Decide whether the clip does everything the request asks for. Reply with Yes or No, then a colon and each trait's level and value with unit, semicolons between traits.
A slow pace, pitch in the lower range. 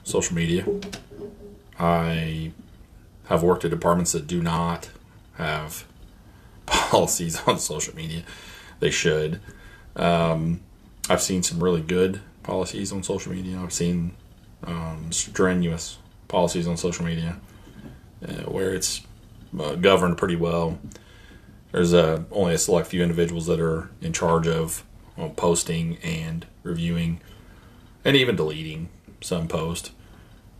Yes: slow, 125 wpm; very low, 85 Hz